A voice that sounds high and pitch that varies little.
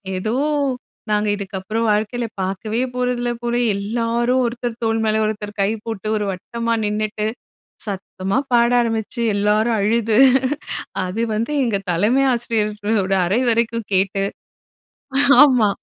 Yes: high, 220 Hz; narrow, 2.3 semitones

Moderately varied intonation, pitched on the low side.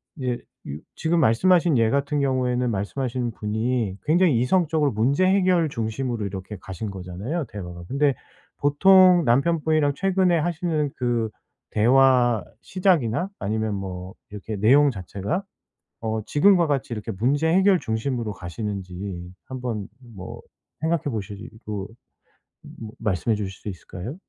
No: wide, 6.6 semitones; low, 125 Hz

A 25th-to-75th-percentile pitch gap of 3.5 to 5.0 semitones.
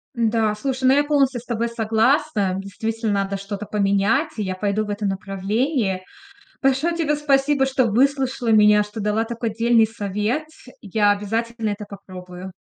Yes: average, 4.2 semitones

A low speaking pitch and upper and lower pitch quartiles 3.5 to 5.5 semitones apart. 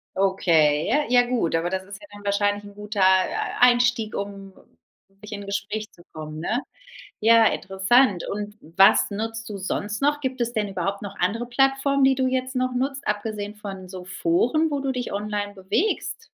No: high, 210 Hz; average, 4.1 semitones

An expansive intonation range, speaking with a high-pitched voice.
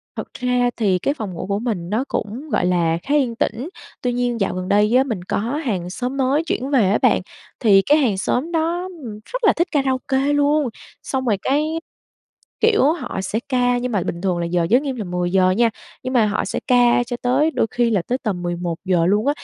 Yes: wide, 5.8 semitones; high, 240 Hz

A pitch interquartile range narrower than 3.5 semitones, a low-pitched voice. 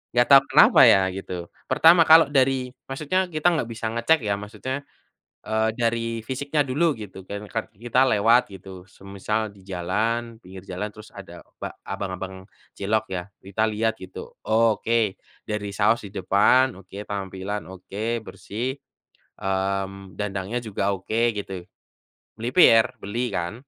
No: average, 3.8 semitones; low, 110 Hz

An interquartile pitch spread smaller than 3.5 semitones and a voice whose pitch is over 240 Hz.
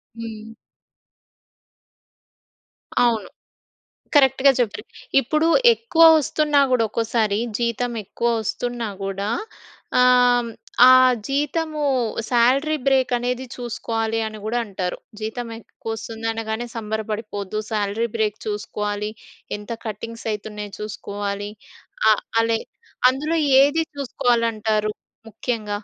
No: average, 2.8 semitones; high, 225 Hz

